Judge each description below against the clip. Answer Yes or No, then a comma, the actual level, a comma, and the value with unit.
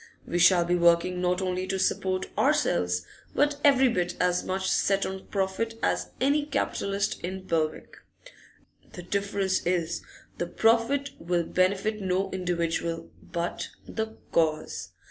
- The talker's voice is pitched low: No, medium, 185 Hz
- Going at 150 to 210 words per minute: No, average, 140 wpm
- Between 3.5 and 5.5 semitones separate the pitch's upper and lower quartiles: No, narrow, 2.5 semitones